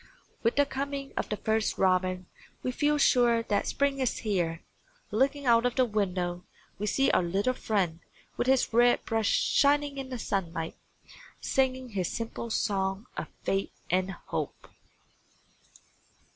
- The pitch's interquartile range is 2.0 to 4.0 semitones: No, average, 5.3 semitones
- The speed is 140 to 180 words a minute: Yes, average, 145 wpm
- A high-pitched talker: Yes, high, 225 Hz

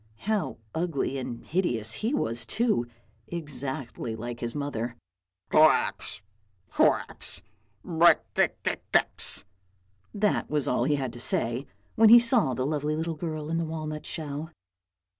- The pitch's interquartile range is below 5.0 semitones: No, wide, 5.5 semitones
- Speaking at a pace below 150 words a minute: Yes, average, 140 wpm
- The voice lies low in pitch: No, medium, 150 Hz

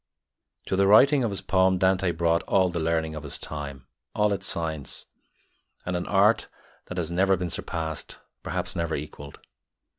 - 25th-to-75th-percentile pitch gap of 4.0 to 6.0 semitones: No, average, 3.2 semitones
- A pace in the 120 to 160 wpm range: No, average, 170 wpm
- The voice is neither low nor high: No, very low, 90 Hz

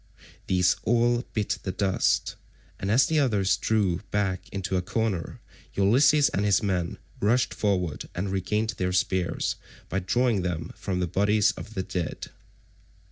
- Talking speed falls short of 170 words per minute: Yes, average, 150 wpm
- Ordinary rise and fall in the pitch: Yes, average, 3.3 semitones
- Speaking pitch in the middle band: No, low, 100 Hz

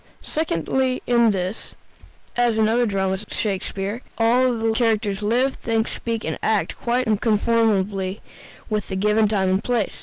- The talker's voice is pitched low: No, high, 220 Hz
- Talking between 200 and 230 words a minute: No, average, 155 wpm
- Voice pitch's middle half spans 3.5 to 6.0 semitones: No, average, 3.0 semitones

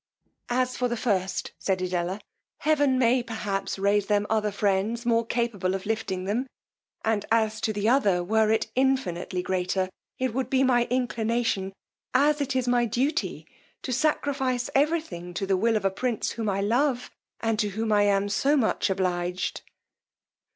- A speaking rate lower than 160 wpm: No, average, 170 wpm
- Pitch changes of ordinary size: Yes, average, 4.3 semitones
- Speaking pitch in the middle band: No, high, 220 Hz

